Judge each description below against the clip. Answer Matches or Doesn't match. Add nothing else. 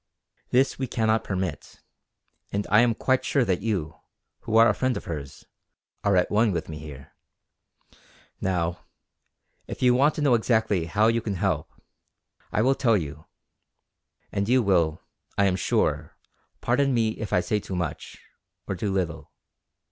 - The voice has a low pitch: Matches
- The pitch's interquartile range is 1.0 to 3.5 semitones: Doesn't match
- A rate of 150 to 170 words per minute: Matches